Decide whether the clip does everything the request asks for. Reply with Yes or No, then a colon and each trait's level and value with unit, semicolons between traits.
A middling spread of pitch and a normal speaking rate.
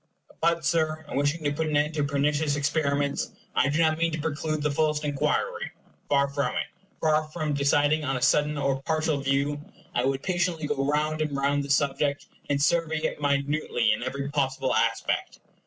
No: narrow, 1.7 semitones; average, 190 wpm